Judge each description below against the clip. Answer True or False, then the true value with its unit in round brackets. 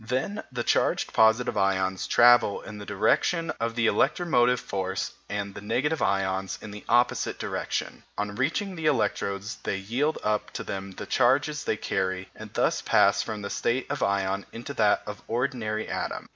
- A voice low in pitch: True (110 Hz)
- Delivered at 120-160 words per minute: False (170 wpm)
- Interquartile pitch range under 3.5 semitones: False (4.3 semitones)